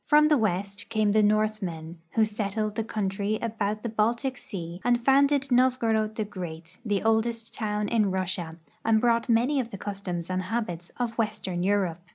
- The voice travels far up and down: No, average, 3.3 semitones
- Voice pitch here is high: Yes, high, 215 Hz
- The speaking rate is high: No, average, 175 wpm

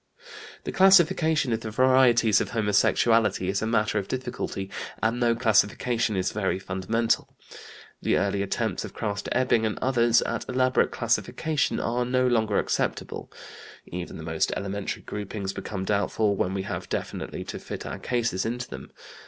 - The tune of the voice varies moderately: Yes, average, 3.6 semitones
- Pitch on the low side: Yes, low, 110 Hz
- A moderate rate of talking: Yes, average, 155 wpm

